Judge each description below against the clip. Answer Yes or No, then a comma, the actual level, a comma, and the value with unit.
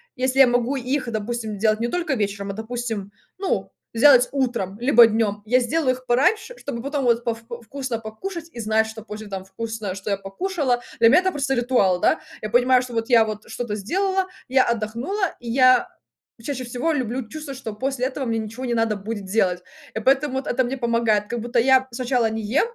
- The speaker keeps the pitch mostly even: No, average, 3.2 semitones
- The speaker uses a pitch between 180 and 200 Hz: No, high, 240 Hz